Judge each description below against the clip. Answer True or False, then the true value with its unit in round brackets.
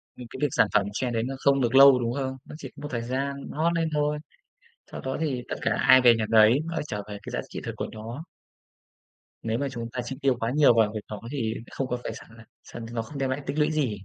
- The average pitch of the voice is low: True (130 Hz)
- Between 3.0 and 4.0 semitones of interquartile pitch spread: True (3.4 semitones)